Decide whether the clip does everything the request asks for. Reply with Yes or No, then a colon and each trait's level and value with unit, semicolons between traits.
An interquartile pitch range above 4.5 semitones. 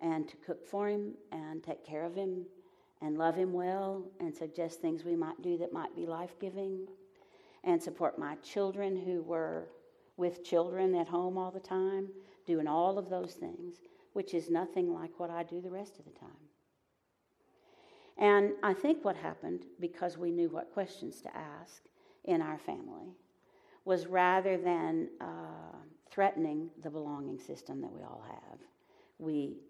No: average, 2.7 semitones